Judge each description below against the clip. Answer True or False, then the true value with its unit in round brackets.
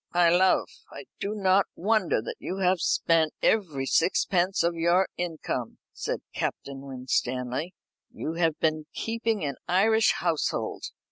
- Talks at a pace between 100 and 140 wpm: True (135 wpm)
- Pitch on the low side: False (170 Hz)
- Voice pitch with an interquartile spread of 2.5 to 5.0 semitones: True (3.8 semitones)